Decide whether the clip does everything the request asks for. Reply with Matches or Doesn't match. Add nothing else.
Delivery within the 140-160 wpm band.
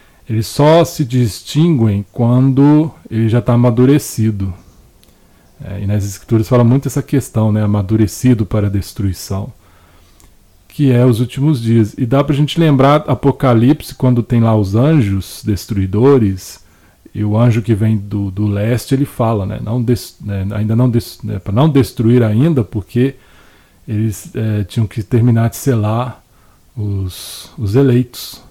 Matches